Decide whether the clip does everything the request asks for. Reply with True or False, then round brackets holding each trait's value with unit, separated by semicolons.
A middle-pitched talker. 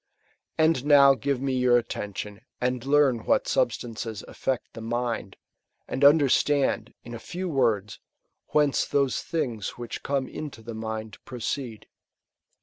False (125 Hz)